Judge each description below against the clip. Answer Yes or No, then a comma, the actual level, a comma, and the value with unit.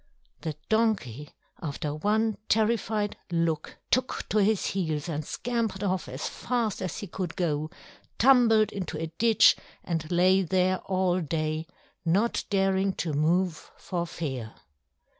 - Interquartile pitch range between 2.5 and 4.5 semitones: No, average, 5.0 semitones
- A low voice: No, medium, 185 Hz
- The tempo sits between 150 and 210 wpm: No, slow, 135 wpm